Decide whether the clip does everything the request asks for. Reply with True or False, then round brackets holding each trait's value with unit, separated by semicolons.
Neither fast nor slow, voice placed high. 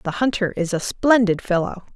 True (185 wpm; 205 Hz)